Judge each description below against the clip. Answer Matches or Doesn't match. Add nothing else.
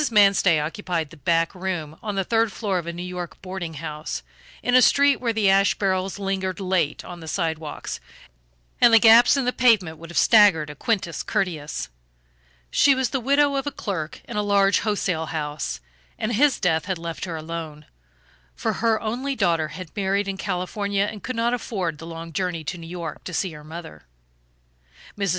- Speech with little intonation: Doesn't match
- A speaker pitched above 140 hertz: Matches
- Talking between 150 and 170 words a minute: Doesn't match